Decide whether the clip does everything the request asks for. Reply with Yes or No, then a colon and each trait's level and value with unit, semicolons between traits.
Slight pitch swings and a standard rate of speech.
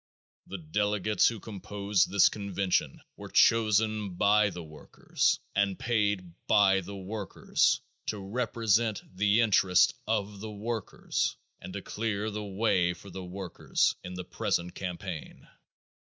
No: narrow, 2.3 semitones; slow, 130 wpm